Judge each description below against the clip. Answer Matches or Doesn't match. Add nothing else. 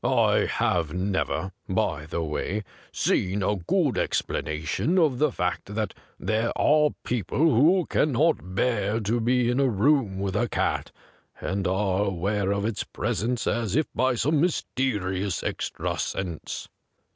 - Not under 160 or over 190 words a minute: Doesn't match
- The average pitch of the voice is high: Doesn't match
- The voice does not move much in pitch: Doesn't match